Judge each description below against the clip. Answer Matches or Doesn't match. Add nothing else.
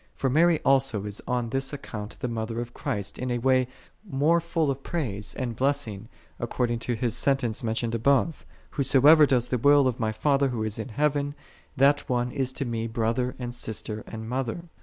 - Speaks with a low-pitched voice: Matches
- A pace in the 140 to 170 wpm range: Doesn't match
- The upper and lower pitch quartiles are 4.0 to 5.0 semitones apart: Doesn't match